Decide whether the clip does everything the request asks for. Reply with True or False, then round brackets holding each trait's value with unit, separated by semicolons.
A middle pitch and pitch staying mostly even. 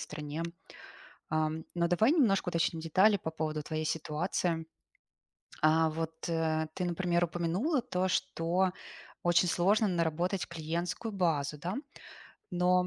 True (170 Hz; 2.2 semitones)